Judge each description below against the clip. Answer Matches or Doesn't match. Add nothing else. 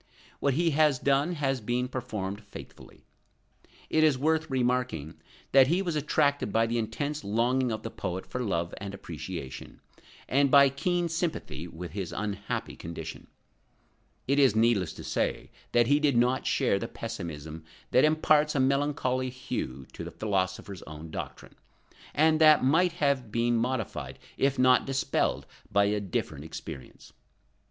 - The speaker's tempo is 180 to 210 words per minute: Doesn't match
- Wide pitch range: Matches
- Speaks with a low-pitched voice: Matches